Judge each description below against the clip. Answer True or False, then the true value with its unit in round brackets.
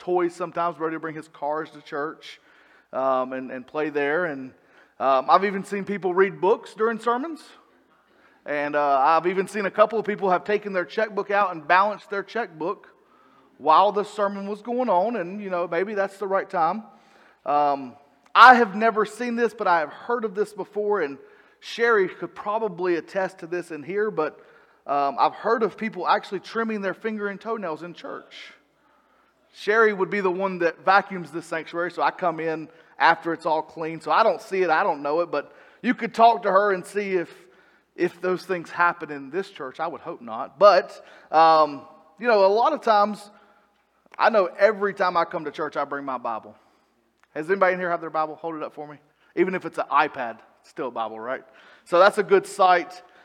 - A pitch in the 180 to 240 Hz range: True (185 Hz)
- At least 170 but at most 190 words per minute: False (205 wpm)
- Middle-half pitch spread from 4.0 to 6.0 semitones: True (4.5 semitones)